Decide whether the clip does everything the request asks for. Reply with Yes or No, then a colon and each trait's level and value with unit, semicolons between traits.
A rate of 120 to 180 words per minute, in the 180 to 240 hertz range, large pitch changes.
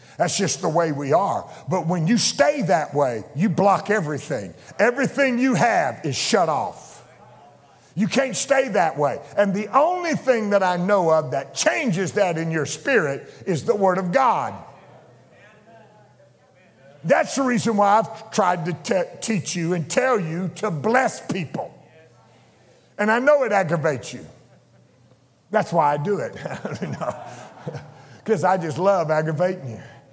Yes: average, 155 wpm; medium, 185 Hz; wide, 5.7 semitones